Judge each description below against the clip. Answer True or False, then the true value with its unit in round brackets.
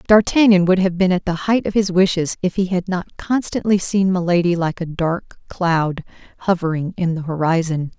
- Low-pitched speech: False (180 Hz)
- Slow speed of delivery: False (190 wpm)